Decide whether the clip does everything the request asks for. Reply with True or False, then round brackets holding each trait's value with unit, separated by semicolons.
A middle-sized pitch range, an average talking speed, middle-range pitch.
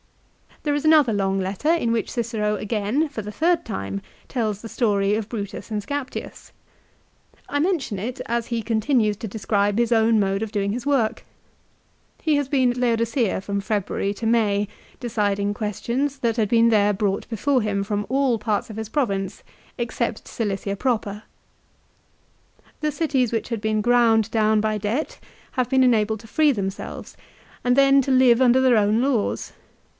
False (3.5 semitones; 175 wpm; 225 Hz)